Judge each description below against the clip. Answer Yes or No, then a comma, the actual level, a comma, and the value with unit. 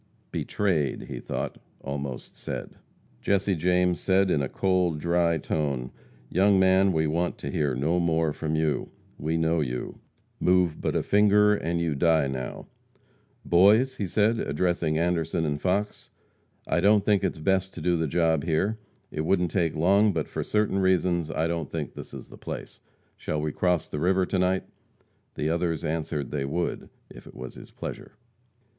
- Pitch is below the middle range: Yes, very low, 85 Hz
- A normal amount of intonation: Yes, average, 3.3 semitones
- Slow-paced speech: No, average, 175 wpm